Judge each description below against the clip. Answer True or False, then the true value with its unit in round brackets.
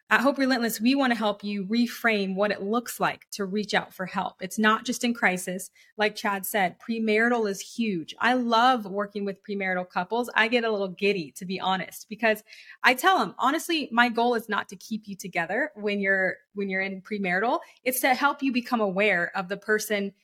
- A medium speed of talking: False (210 wpm)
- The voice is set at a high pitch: True (210 Hz)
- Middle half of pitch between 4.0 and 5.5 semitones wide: False (3.5 semitones)